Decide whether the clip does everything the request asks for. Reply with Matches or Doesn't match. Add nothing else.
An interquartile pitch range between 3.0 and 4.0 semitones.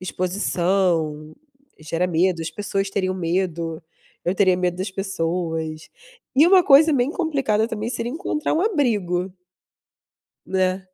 Doesn't match